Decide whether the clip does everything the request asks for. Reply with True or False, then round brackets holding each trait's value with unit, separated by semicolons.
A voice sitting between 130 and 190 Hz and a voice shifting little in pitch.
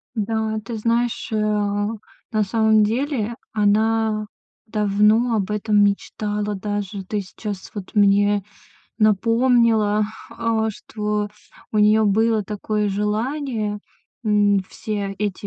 False (210 Hz; 1.3 semitones)